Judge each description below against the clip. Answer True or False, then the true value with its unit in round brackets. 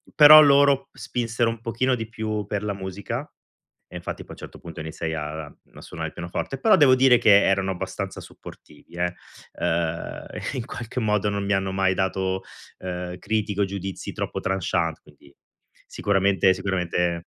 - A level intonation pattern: False (4.4 semitones)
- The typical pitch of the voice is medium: False (95 Hz)